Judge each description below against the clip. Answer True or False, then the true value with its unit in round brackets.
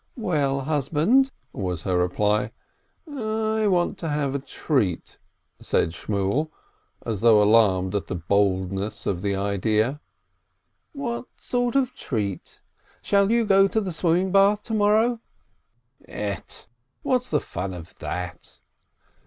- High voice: False (135 Hz)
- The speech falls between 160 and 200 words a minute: False (135 wpm)